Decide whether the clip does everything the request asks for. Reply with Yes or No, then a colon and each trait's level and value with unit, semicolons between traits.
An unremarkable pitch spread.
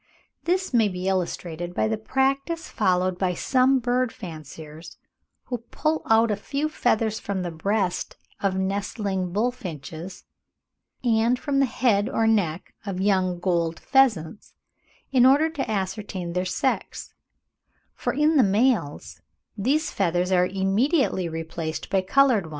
No: wide, 5.8 semitones